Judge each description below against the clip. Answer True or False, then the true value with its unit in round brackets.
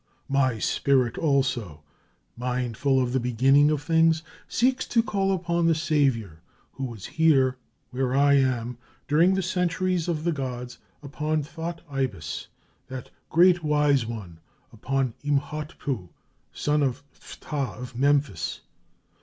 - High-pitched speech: False (140 Hz)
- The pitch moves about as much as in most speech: True (4.3 semitones)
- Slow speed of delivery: True (130 wpm)